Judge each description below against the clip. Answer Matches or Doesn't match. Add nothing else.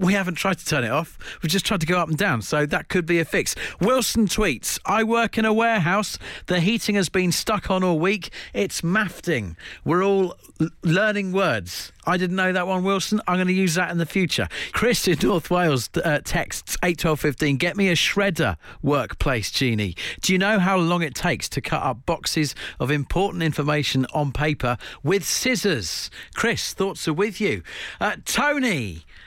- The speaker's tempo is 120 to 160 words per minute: Doesn't match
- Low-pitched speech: Doesn't match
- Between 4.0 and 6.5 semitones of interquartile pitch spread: Matches